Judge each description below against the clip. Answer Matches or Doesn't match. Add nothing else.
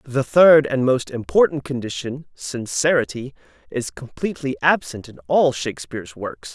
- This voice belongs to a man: Matches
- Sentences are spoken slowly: Matches